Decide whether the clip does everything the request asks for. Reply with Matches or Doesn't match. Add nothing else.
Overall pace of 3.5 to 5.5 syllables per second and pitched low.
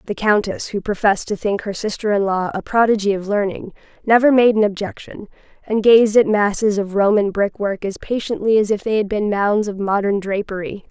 Doesn't match